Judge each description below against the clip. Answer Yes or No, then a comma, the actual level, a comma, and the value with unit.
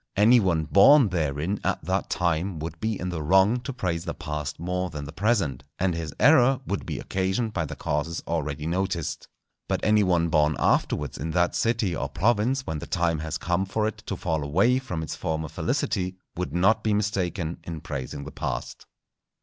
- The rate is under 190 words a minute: No, average, 195 wpm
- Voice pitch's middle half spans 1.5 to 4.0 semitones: No, average, 4.6 semitones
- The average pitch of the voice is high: No, very low, 90 Hz